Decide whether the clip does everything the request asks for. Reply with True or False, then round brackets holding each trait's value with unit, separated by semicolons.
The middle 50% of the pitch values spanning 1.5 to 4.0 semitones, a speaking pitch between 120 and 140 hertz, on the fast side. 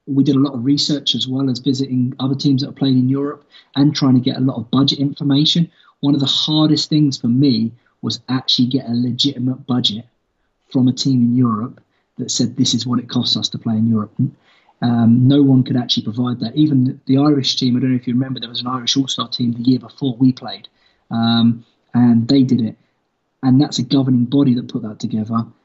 True (2.4 semitones; 130 Hz; 230 wpm)